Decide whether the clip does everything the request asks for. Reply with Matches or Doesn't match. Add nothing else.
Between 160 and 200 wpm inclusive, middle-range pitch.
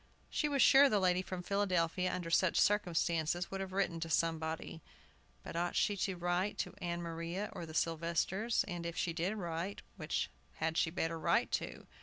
Matches